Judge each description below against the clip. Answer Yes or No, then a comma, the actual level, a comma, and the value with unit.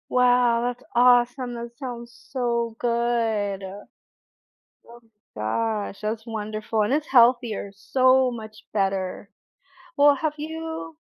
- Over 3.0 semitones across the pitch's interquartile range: No, average, 2.7 semitones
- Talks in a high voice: Yes, high, 235 Hz